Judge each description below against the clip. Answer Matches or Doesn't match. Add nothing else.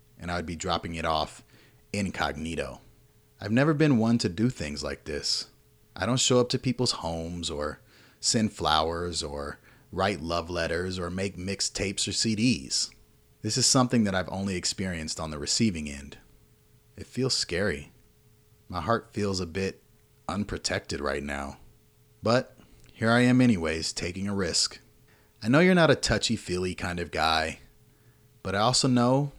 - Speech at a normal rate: Matches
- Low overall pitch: Matches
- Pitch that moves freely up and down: Matches